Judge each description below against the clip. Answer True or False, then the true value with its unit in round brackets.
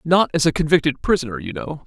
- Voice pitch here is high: False (155 Hz)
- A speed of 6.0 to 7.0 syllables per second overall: True (6.3 syllables/s)